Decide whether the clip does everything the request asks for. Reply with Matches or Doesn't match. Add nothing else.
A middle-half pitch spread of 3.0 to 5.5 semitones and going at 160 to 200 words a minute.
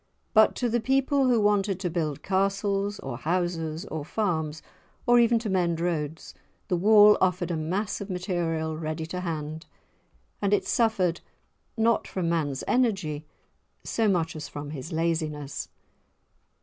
Doesn't match